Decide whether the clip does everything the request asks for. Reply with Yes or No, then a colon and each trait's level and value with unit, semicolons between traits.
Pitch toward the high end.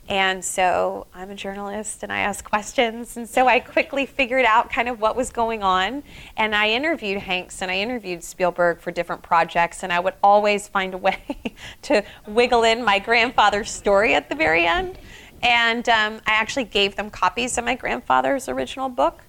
Yes: high, 205 Hz